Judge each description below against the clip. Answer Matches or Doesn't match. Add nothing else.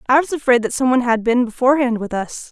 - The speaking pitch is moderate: Doesn't match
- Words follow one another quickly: Matches